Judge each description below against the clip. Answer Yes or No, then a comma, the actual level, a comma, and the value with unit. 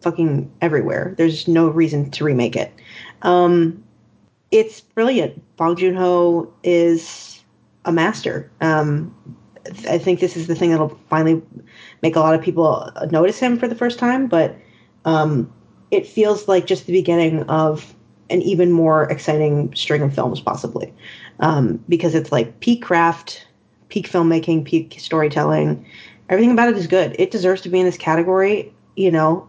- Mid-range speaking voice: Yes, medium, 165 Hz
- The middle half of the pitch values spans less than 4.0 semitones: Yes, average, 2.9 semitones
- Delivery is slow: No, average, 160 wpm